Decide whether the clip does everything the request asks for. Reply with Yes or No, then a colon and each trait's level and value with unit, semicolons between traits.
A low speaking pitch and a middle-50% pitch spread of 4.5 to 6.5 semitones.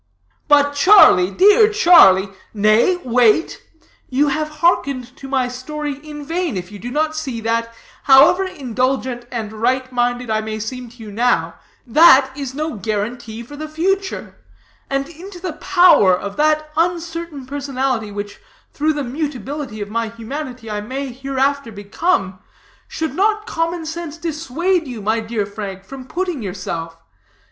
No: very high, 265 Hz; wide, 5.6 semitones